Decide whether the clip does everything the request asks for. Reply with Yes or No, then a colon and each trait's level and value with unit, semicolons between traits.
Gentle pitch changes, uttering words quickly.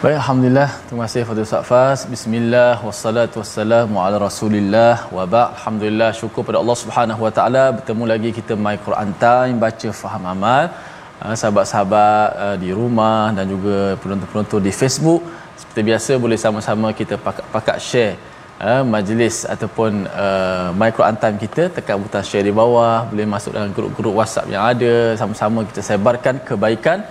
Yes: narrow, 2.2 semitones; fast, 145 wpm